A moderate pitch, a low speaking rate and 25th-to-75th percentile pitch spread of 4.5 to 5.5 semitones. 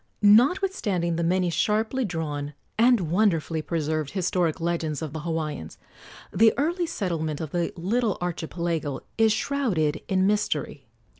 Yes: medium, 175 Hz; slow, 130 wpm; average, 5.2 semitones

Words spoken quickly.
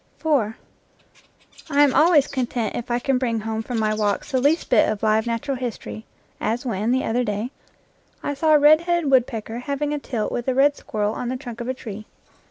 Yes: fast, 210 wpm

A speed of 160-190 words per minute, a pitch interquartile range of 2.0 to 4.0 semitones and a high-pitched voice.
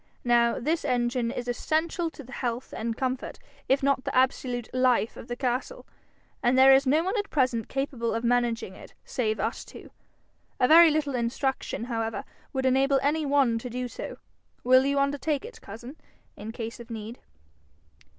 Yes: average, 180 wpm; average, 2.8 semitones; very high, 255 Hz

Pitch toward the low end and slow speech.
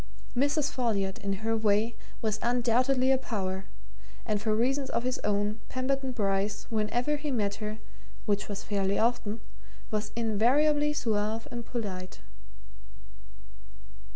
No: high, 225 Hz; slow, 125 wpm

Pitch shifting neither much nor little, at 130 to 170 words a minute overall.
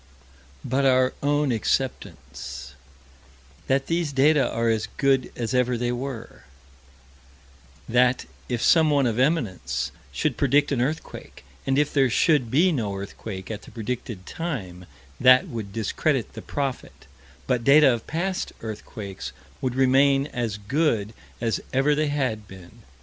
Yes: average, 4.2 semitones; average, 140 wpm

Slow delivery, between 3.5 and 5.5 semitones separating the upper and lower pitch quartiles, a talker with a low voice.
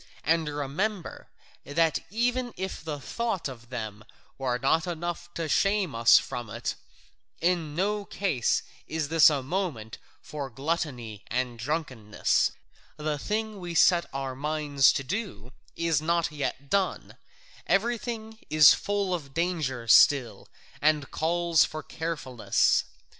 No: slow, 130 wpm; average, 5.0 semitones; medium, 155 Hz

